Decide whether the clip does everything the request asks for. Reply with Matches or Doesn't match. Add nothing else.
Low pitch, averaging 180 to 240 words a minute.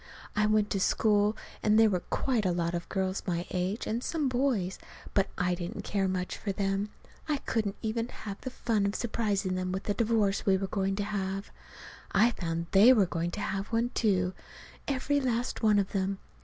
Doesn't match